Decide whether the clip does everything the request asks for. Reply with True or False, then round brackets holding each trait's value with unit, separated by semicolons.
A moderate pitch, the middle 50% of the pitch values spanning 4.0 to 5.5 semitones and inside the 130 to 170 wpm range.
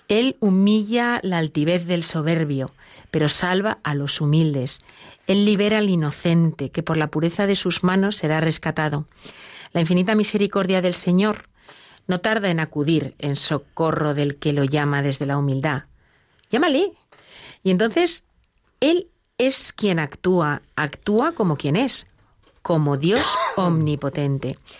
True (165 Hz; 5.1 semitones; 135 wpm)